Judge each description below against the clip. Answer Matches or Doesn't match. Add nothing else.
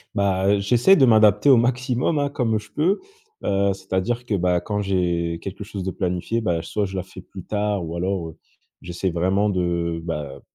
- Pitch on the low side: Matches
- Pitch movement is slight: Doesn't match